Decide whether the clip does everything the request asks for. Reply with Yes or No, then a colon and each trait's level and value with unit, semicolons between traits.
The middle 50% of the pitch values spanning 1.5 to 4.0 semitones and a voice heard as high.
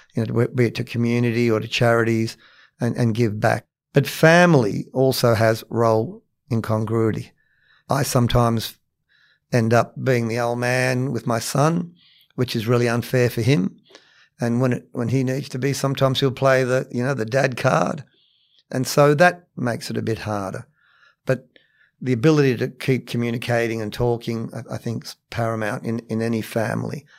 No: narrow, 2.4 semitones; low, 120 Hz